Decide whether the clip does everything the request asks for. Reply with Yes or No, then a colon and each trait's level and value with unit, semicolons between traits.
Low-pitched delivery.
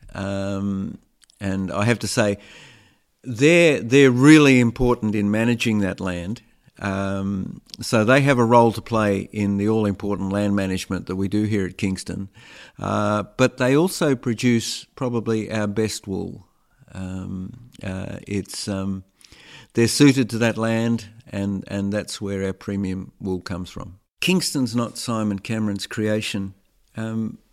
Yes: low, 105 Hz